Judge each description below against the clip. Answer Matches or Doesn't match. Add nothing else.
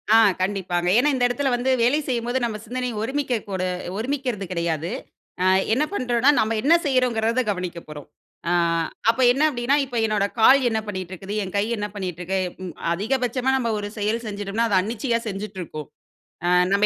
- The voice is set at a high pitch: Matches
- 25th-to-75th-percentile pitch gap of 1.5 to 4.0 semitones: Doesn't match